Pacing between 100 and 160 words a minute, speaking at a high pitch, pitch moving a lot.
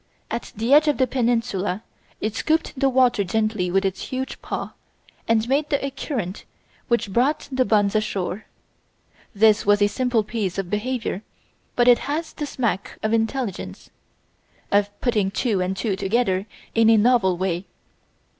No: average, 155 wpm; high, 220 Hz; average, 4.3 semitones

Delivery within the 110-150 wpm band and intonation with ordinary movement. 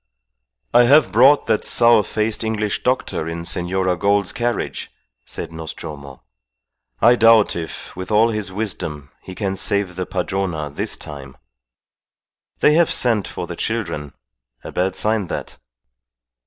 Yes: average, 140 wpm; average, 4.8 semitones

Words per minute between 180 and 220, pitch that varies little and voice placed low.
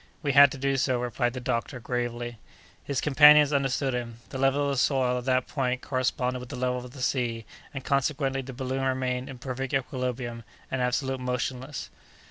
Yes: average, 190 wpm; narrow, 1.4 semitones; low, 130 Hz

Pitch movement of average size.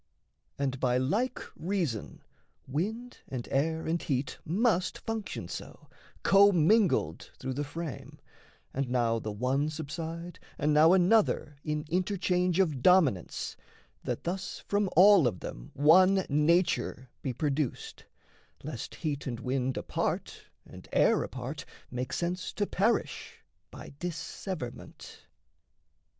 No: wide, 5.8 semitones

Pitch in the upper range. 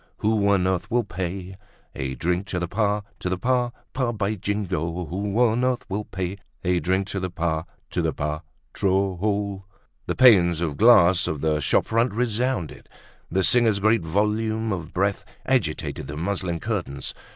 No: very low, 95 Hz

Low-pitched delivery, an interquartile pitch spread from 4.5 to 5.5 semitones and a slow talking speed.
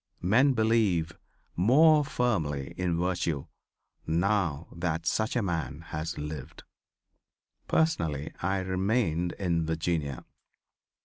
Yes: very low, 85 Hz; average, 5.1 semitones; slow, 100 wpm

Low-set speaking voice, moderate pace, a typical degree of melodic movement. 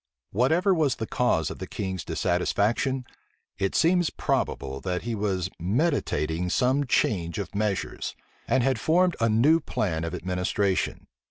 No: low, 105 Hz; average, 145 wpm; wide, 6.6 semitones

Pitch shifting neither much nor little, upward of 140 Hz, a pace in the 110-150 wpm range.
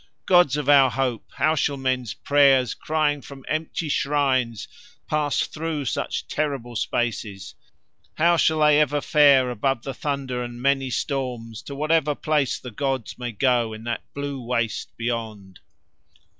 No: average, 3.4 semitones; low, 135 Hz; average, 145 wpm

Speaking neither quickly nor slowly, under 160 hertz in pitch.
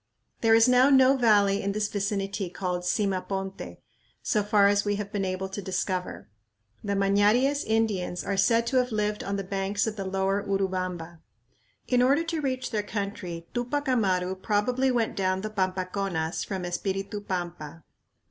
No: average, 165 wpm; high, 200 Hz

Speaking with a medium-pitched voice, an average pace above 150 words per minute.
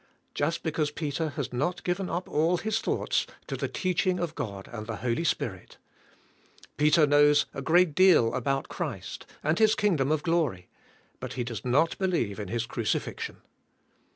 Yes: medium, 150 Hz; average, 165 wpm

